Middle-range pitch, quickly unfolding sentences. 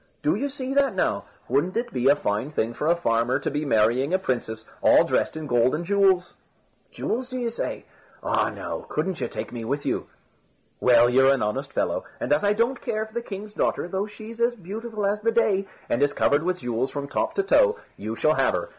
Yes: medium, 180 Hz; fast, 225 wpm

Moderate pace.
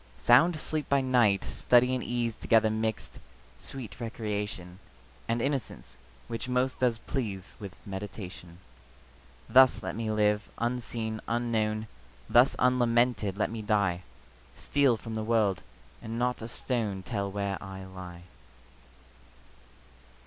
No: slow, 125 wpm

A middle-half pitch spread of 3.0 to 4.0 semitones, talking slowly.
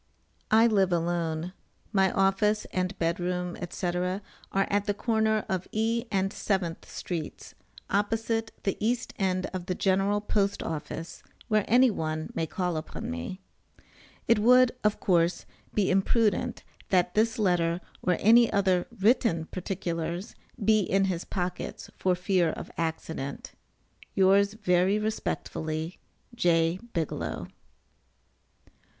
Yes: average, 3.4 semitones; slow, 125 wpm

